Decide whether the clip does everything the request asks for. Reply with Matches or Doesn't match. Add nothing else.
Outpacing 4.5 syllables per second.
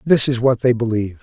Matches